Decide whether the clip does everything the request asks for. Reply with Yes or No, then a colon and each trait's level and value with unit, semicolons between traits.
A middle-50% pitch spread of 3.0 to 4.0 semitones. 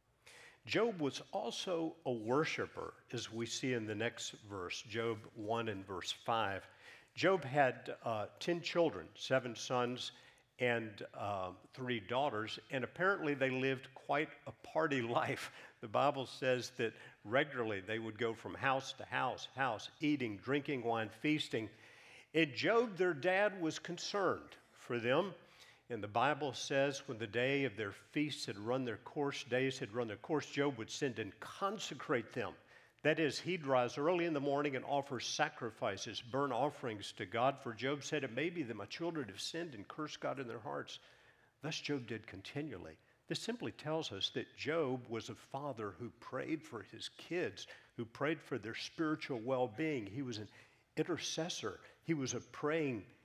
No: average, 4.5 semitones